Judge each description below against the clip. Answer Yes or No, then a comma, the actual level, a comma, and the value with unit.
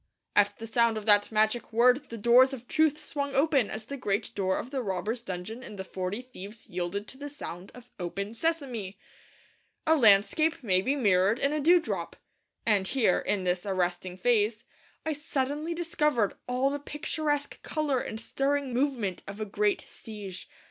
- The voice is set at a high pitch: Yes, high, 230 Hz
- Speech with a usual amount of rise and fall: No, wide, 5.7 semitones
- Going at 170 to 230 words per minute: Yes, average, 175 wpm